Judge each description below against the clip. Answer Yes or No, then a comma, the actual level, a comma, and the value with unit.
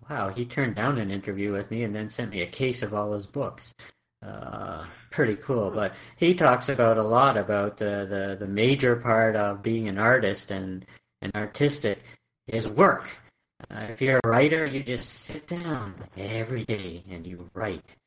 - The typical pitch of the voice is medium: No, low, 110 Hz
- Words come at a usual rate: Yes, average, 185 wpm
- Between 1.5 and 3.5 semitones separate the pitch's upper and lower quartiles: No, average, 4.0 semitones